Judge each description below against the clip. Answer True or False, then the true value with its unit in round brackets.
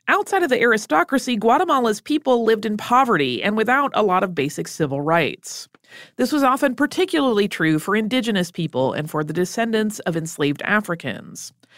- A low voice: False (220 Hz)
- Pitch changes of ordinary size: False (6.8 semitones)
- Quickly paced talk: False (165 wpm)